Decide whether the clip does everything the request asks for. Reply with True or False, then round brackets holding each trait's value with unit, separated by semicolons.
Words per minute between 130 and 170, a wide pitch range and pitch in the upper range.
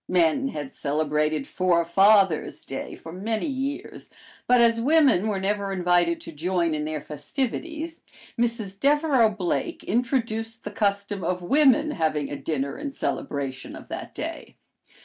True (140 wpm; 6.9 semitones; 195 Hz)